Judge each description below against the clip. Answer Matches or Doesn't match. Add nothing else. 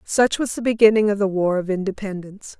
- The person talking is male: Doesn't match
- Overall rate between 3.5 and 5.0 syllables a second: Doesn't match